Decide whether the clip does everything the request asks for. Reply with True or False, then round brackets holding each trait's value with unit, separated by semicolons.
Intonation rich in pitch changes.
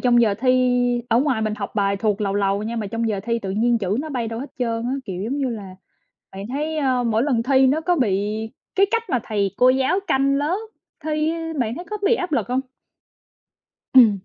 False (4.4 semitones)